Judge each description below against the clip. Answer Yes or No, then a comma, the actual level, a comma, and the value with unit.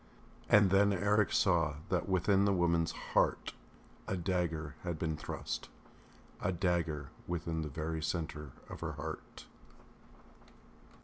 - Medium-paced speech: No, slow, 125 wpm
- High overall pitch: No, very low, 85 Hz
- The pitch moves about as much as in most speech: Yes, average, 3.0 semitones